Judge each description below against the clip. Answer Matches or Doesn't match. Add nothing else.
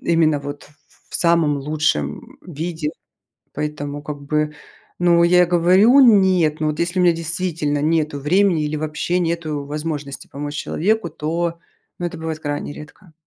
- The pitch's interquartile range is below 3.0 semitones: Matches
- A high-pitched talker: Doesn't match